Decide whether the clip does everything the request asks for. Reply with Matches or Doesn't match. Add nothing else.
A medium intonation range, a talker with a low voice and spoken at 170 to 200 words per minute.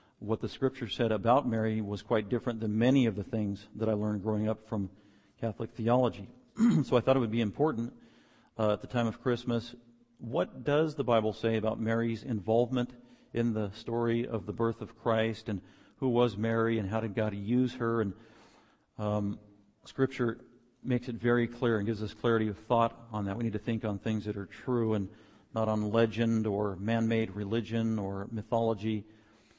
Doesn't match